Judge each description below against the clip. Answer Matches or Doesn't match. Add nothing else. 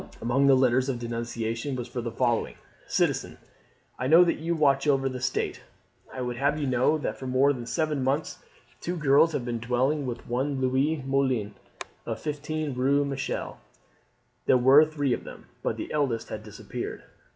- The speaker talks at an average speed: Matches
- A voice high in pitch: Doesn't match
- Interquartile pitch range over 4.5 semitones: Doesn't match